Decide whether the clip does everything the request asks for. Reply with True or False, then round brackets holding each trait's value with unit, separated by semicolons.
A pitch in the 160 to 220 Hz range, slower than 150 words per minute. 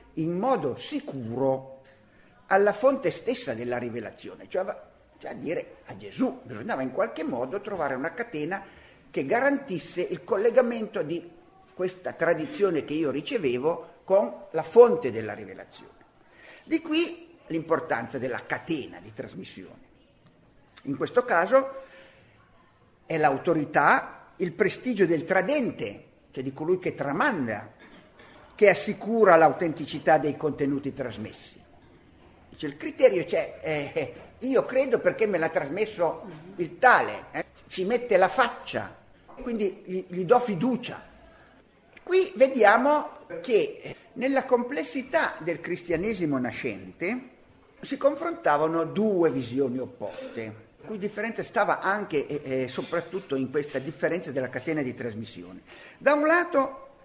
True (185 Hz; 125 wpm)